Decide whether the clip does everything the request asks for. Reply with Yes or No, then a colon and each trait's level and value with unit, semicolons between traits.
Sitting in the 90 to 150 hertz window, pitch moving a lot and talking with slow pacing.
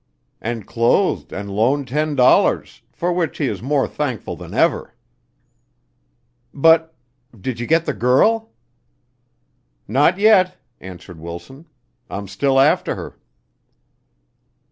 Yes: low, 135 Hz; wide, 6.4 semitones; slow, 115 wpm